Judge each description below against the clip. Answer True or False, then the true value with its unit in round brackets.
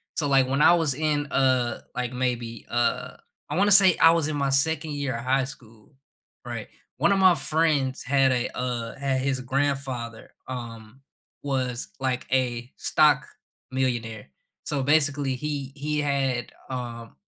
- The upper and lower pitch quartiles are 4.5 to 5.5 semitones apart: False (2.8 semitones)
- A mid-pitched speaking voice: False (130 Hz)